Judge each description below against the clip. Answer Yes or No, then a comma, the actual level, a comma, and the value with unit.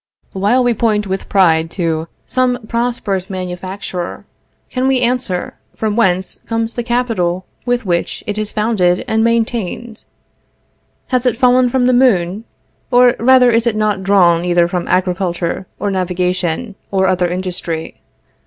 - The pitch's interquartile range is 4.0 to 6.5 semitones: Yes, average, 4.9 semitones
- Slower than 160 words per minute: Yes, average, 145 wpm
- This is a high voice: Yes, high, 205 Hz